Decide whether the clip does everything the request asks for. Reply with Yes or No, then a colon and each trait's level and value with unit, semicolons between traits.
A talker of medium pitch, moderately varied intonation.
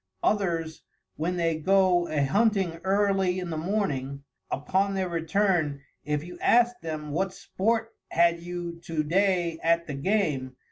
Yes: medium, 175 Hz; average, 3.5 semitones